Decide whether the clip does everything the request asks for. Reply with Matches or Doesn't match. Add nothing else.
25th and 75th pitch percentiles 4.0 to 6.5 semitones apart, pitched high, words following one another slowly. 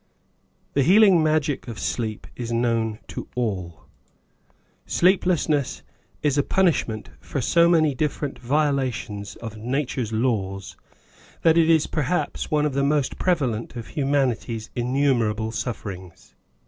Doesn't match